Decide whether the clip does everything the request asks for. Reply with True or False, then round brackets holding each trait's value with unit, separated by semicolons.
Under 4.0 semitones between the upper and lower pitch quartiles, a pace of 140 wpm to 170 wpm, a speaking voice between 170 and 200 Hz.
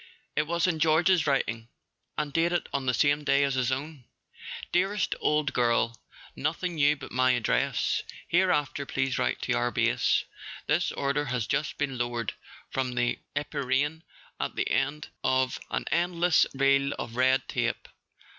False (3.4 semitones; 155 wpm; 140 Hz)